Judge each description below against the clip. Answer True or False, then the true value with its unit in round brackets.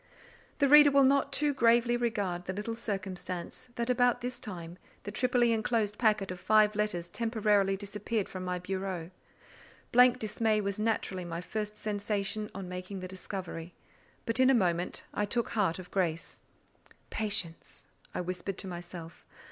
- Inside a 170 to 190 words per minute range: False (155 wpm)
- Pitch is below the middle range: False (205 Hz)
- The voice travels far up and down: False (4.0 semitones)